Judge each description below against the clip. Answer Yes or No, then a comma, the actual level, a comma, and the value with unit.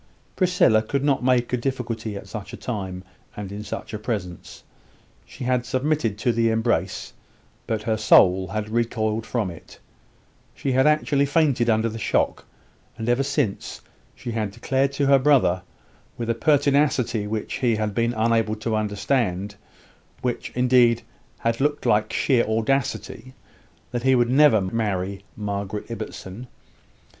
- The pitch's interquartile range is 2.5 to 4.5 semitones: Yes, average, 3.3 semitones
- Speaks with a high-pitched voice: No, low, 115 Hz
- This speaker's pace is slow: No, average, 150 wpm